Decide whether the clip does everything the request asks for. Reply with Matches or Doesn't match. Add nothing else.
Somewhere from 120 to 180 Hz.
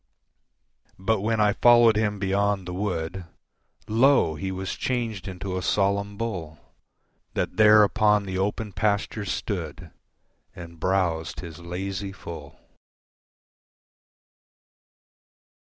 Doesn't match